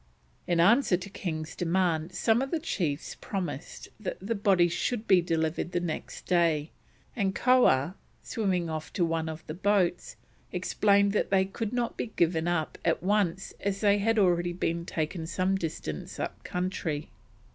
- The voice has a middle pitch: Yes, medium, 180 Hz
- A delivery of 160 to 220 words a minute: Yes, average, 165 wpm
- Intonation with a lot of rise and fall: No, average, 3.5 semitones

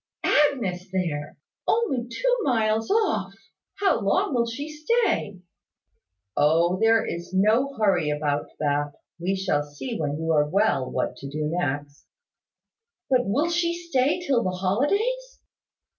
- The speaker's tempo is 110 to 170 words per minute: Yes, slow, 135 wpm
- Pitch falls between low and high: No, high, 205 Hz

